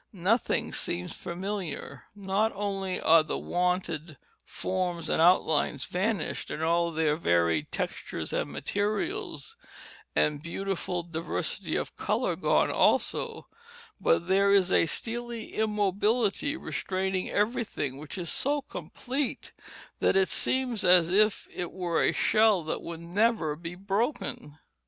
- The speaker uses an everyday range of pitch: Yes, average, 4.1 semitones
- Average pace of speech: No, slow, 125 wpm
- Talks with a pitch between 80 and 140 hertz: No, medium, 185 Hz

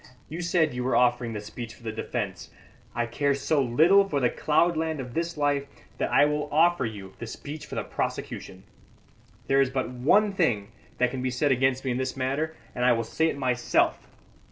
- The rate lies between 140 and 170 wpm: No, fast, 205 wpm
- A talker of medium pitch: No, low, 130 Hz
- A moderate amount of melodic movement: Yes, average, 4.2 semitones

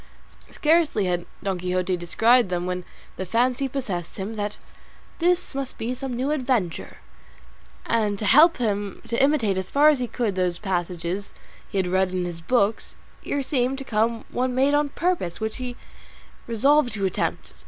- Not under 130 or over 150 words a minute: No, average, 175 wpm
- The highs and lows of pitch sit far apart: Yes, wide, 6.0 semitones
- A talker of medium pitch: No, high, 225 Hz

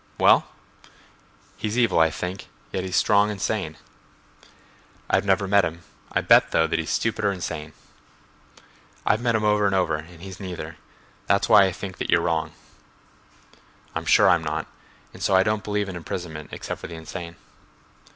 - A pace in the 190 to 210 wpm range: No, average, 170 wpm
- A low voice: Yes, very low, 95 Hz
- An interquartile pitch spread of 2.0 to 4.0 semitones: Yes, average, 3.7 semitones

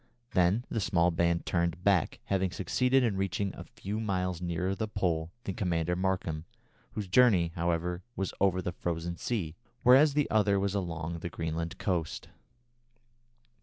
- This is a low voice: Yes, very low, 90 Hz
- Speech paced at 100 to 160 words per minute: Yes, average, 155 wpm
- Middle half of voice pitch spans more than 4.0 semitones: No, average, 2.8 semitones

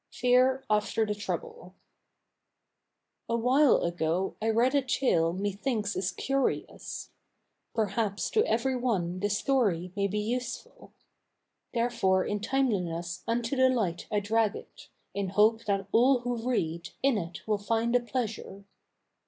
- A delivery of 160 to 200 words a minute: No, slow, 135 wpm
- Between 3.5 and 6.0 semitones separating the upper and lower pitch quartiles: Yes, average, 4.1 semitones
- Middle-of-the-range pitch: No, high, 220 Hz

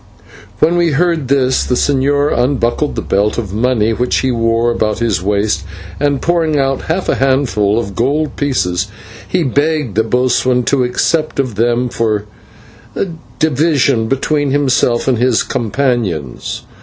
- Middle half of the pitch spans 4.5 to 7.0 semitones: No, average, 3.9 semitones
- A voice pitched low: Yes, low, 125 Hz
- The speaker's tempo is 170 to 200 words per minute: No, average, 145 wpm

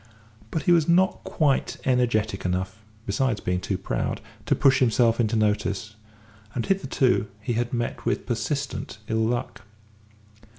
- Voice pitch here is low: Yes, low, 115 Hz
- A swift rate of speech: No, average, 140 wpm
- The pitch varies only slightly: No, average, 3.8 semitones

